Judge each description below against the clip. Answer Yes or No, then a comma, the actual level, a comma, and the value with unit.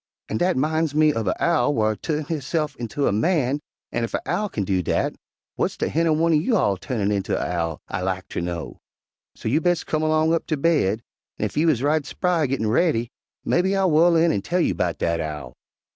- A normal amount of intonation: No, wide, 8.0 semitones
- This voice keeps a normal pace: No, fast, 225 wpm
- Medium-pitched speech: Yes, medium, 145 Hz